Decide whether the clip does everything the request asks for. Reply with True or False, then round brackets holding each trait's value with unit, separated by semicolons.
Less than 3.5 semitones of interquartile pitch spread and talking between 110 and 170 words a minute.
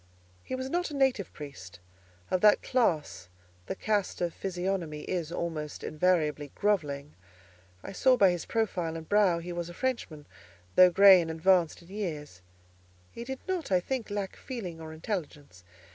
False (4.8 semitones; 160 wpm)